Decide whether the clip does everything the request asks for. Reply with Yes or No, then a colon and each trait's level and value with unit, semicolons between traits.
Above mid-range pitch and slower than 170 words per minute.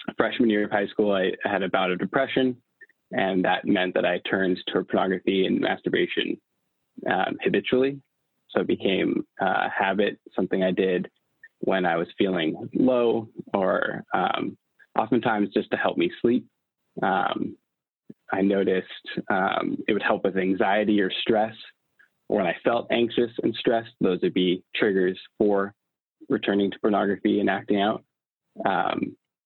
No: low, 105 Hz; average, 150 wpm